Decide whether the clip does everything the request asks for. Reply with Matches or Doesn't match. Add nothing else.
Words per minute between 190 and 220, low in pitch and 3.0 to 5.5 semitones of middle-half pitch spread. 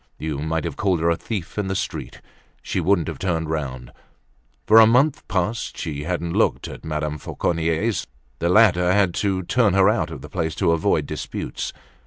Matches